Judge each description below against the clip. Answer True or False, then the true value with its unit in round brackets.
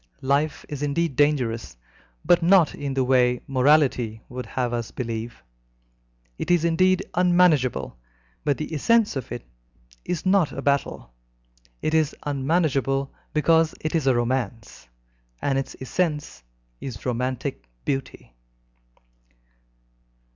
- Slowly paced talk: True (120 wpm)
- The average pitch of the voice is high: False (140 Hz)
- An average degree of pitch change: True (4.2 semitones)